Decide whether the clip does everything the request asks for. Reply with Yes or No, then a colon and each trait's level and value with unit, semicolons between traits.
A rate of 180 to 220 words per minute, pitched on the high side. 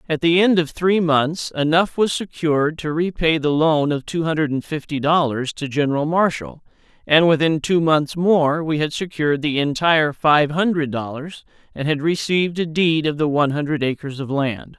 No: average, 190 wpm; medium, 155 Hz